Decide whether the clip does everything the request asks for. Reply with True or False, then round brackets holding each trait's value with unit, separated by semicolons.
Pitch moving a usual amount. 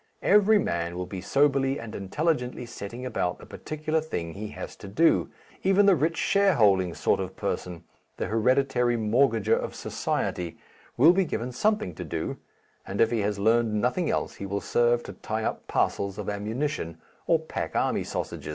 False (6.9 semitones)